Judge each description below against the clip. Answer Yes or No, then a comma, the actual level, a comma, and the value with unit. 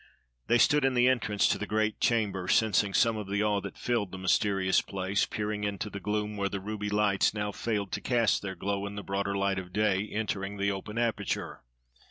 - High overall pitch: No, low, 105 Hz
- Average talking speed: No, fast, 215 wpm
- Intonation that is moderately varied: No, narrow, 1.5 semitones